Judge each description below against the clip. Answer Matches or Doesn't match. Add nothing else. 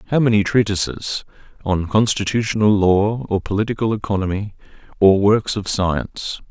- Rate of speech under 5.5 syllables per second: Matches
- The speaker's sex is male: Matches